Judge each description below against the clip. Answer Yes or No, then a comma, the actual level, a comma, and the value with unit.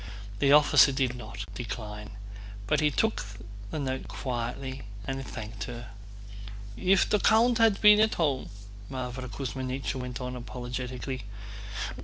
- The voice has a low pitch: Yes, low, 130 Hz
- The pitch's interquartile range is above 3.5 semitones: No, narrow, 2.5 semitones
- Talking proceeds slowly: Yes, slow, 125 wpm